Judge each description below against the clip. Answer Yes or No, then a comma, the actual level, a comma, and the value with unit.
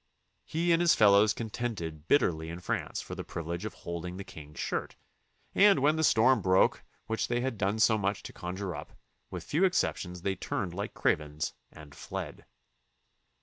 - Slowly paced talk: No, average, 180 wpm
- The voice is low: Yes, low, 100 Hz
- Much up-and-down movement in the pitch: Yes, wide, 6.0 semitones